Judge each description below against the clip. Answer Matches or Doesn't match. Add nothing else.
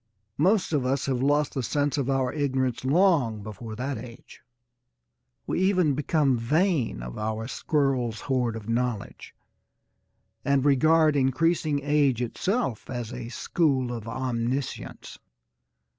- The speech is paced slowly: Matches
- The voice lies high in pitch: Doesn't match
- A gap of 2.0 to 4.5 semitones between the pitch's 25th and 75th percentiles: Matches